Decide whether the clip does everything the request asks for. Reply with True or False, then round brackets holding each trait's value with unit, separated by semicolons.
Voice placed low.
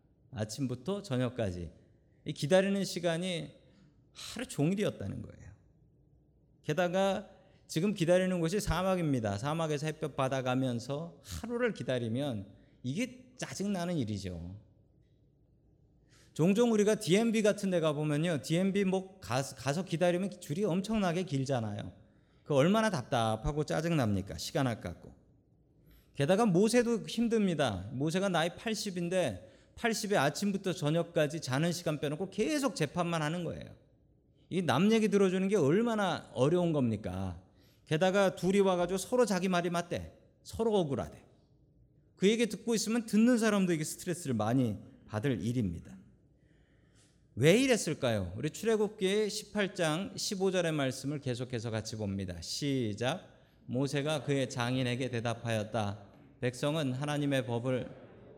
False (150 Hz)